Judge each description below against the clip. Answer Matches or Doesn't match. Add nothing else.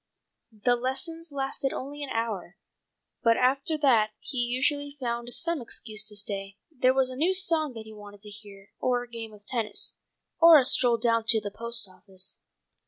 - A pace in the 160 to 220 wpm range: Matches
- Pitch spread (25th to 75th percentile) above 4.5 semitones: Doesn't match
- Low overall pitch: Doesn't match